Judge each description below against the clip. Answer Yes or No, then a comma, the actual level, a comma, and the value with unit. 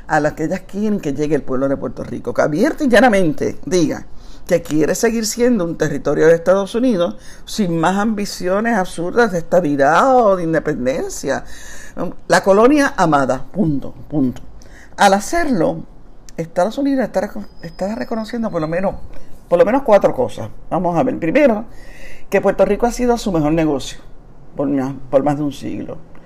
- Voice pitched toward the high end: No, medium, 180 Hz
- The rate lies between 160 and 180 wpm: Yes, average, 170 wpm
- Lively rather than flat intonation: Yes, wide, 6.9 semitones